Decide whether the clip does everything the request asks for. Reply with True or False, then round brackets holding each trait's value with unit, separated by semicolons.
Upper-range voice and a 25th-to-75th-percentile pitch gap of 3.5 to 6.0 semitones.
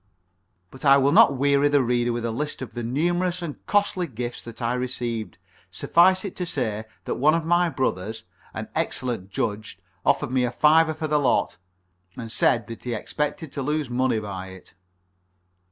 False (130 Hz; 4.6 semitones)